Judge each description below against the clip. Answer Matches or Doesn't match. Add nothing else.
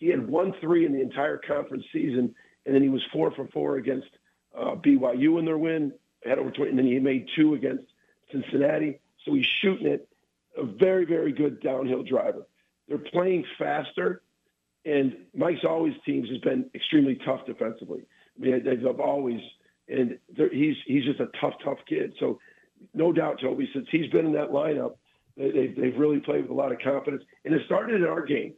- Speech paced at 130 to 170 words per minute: Doesn't match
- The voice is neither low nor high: Matches